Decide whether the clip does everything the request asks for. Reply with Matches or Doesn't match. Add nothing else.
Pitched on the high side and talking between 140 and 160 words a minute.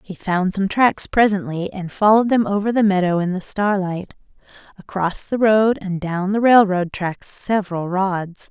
Doesn't match